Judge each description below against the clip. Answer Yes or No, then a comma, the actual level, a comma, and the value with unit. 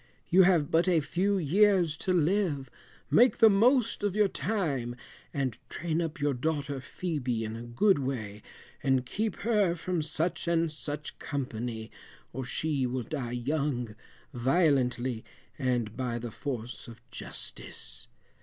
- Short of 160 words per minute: Yes, average, 145 wpm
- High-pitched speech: No, medium, 145 Hz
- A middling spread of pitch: No, wide, 6.2 semitones